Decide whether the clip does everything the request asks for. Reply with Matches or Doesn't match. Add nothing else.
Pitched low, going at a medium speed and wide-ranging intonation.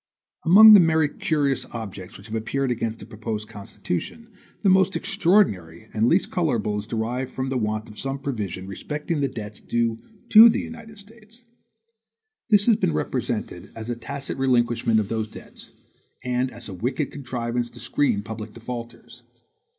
Matches